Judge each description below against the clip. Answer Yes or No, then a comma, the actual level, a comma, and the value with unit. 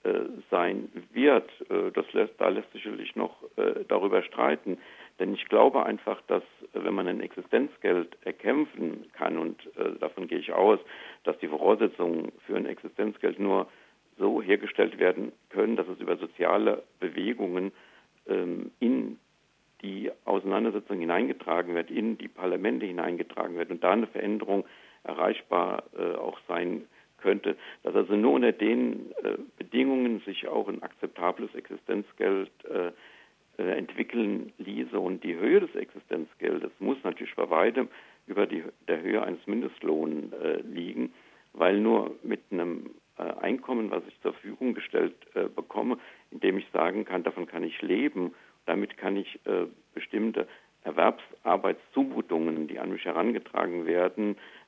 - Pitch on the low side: No, very high, 375 Hz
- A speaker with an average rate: Yes, average, 140 wpm